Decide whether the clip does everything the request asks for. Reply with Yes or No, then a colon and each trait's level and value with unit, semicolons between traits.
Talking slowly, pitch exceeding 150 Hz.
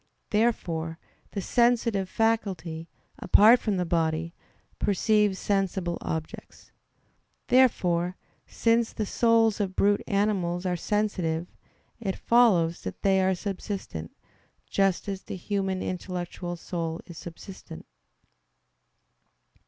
Yes: slow, 105 wpm; high, 190 Hz